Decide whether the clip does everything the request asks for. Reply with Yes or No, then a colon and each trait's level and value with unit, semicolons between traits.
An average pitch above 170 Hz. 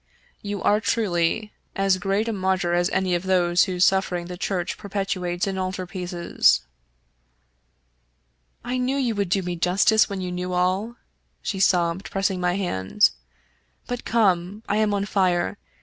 Yes: medium, 185 Hz